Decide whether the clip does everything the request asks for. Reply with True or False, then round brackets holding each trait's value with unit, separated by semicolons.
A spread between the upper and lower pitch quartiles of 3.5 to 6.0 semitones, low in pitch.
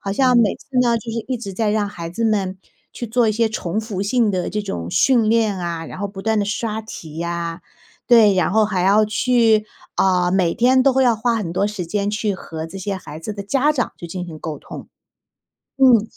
False (3.9 semitones; 210 Hz)